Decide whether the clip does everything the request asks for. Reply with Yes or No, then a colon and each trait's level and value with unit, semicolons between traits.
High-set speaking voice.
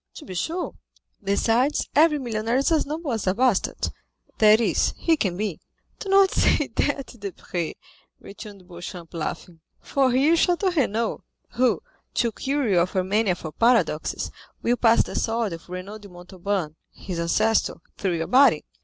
Yes: high, 220 Hz